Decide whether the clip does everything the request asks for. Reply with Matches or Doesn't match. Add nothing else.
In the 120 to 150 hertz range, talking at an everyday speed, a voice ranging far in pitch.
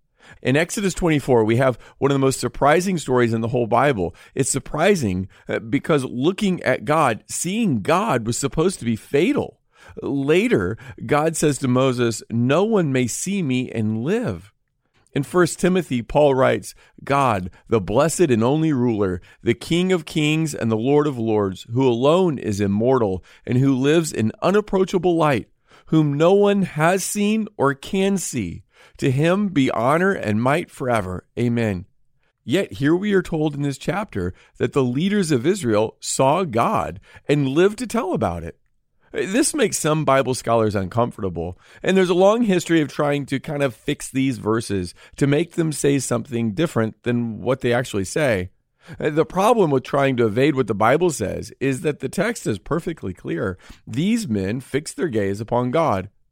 Matches